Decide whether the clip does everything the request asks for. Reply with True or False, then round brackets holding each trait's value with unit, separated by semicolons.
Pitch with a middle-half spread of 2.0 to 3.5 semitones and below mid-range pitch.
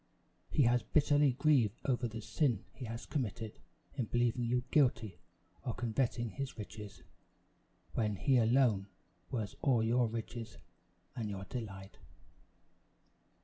True (2.8 semitones; 120 Hz)